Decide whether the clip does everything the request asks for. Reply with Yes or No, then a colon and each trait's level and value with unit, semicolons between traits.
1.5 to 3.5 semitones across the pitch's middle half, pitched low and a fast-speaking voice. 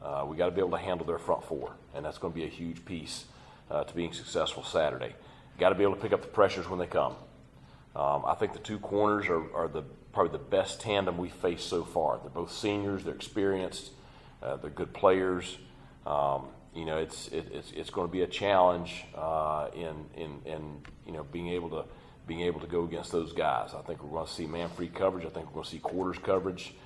Yes: average, 2.8 semitones; very low, 85 Hz; fast, 240 wpm